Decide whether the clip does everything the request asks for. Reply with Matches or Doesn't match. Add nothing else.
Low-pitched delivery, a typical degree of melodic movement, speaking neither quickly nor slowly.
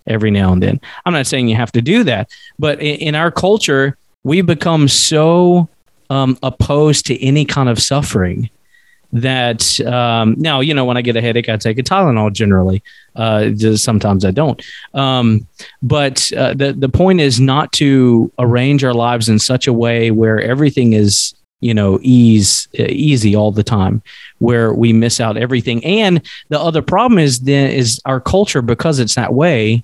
Matches